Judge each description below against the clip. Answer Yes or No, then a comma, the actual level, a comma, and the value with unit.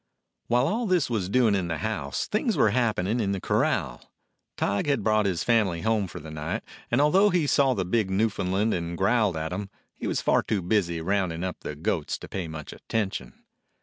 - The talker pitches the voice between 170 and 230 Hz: No, low, 100 Hz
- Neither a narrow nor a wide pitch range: Yes, average, 5.0 semitones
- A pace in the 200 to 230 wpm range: Yes, fast, 205 wpm